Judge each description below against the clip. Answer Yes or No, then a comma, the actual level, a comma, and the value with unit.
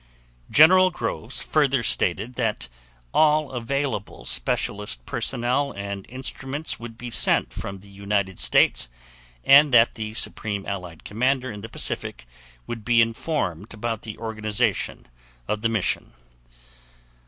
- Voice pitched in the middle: No, low, 115 Hz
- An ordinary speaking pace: No, slow, 125 wpm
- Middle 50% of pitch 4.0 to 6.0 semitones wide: Yes, average, 4.5 semitones